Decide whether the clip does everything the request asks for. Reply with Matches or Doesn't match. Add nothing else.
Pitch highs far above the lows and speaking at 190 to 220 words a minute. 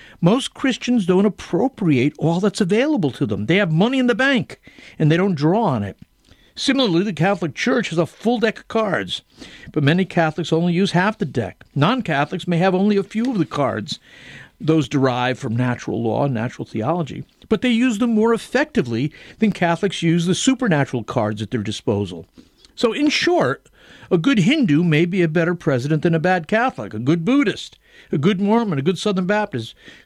Matches